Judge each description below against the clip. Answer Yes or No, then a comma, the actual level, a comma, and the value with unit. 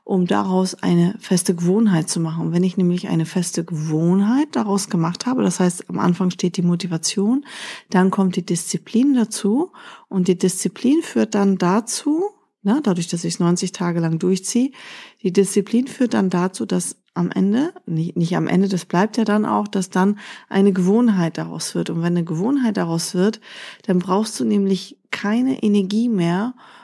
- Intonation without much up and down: No, average, 3.5 semitones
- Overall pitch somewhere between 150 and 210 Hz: Yes, high, 190 Hz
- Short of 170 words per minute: No, average, 180 wpm